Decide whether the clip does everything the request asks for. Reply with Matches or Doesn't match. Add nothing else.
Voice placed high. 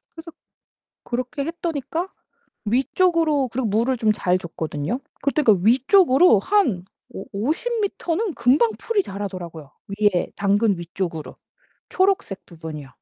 Matches